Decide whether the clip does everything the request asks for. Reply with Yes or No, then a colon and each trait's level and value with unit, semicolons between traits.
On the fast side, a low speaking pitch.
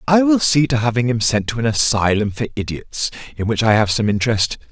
Yes: fast, 230 wpm; low, 115 Hz